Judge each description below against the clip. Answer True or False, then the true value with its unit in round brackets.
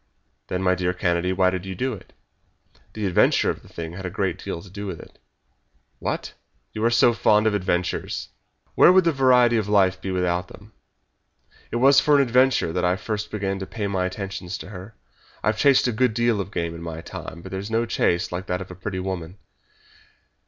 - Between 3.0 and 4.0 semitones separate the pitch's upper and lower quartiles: True (3.4 semitones)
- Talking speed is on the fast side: True (215 wpm)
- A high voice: False (95 Hz)